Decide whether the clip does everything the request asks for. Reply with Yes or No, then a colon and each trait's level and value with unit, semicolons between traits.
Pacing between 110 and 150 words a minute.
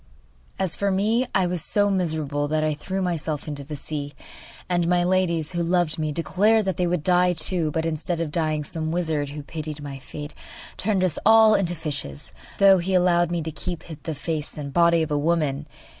No: fast, 205 wpm